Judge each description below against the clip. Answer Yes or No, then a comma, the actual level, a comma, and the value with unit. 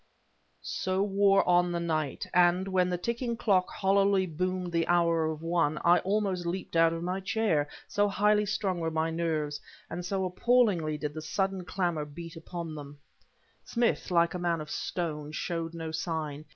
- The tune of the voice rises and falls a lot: No, average, 2.9 semitones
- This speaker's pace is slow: No, average, 175 wpm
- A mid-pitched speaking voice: Yes, medium, 175 Hz